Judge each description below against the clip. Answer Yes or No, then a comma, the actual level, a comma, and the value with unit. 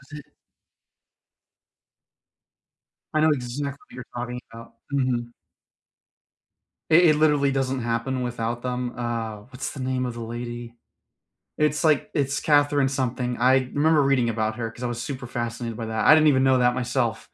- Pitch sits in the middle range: No, low, 125 Hz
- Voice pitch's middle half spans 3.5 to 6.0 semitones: No, average, 2.9 semitones